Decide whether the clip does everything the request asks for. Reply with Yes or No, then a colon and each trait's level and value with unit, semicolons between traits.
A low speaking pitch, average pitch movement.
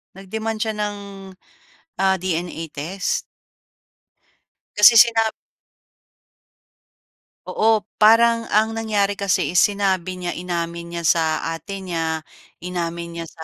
No: high, 190 Hz; average, 4.0 semitones